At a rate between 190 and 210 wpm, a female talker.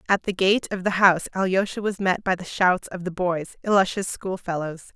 Yes: fast, 205 wpm; female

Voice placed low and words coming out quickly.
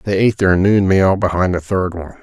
Yes: very low, 95 Hz; fast, 245 wpm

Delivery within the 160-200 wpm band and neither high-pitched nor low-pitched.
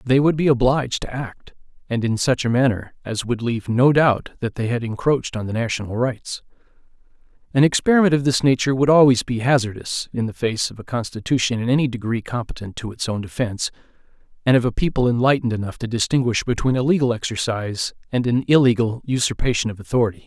No: average, 190 wpm; low, 120 Hz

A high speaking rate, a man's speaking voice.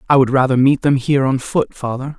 Yes: fast, 245 wpm; male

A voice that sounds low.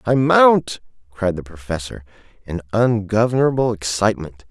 Yes: low, 105 Hz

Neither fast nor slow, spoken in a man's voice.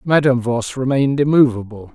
No: slow, 125 wpm; male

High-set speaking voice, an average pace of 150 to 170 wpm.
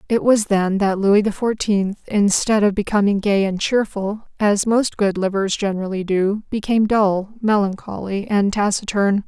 Yes: high, 205 Hz; average, 155 wpm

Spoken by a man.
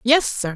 No: female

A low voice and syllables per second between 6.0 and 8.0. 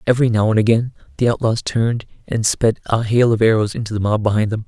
Yes: low, 110 Hz; 6.5 syllables/s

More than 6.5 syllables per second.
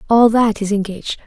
No: 5.8 syllables/s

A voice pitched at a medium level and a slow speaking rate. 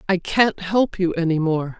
No: medium, 180 Hz; average, 200 wpm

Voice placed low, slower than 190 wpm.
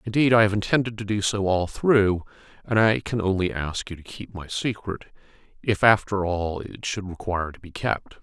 No: low, 100 Hz; fast, 205 wpm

